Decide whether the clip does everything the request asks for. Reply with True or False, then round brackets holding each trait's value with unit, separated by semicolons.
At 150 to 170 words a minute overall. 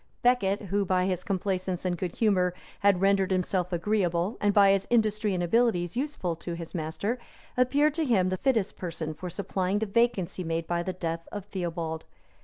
False (185 wpm)